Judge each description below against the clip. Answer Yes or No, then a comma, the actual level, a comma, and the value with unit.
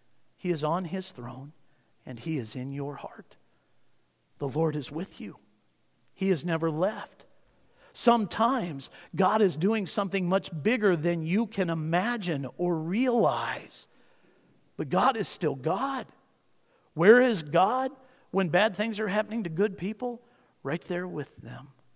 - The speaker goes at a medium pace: Yes, average, 145 wpm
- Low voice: No, medium, 180 Hz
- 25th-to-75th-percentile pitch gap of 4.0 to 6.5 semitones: Yes, wide, 5.4 semitones